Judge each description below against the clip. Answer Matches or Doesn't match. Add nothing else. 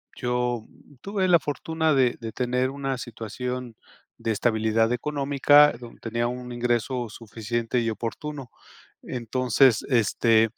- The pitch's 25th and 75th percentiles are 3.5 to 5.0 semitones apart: Doesn't match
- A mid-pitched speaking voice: Doesn't match